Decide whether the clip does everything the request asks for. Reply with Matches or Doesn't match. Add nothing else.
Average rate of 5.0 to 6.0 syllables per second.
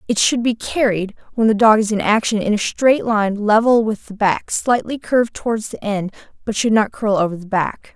Matches